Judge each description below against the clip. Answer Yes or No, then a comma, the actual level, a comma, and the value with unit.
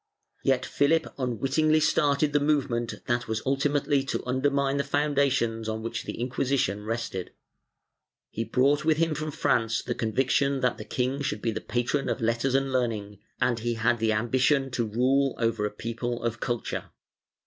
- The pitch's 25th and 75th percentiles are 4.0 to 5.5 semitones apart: No, average, 3.3 semitones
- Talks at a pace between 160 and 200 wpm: Yes, average, 170 wpm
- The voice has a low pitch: Yes, low, 125 Hz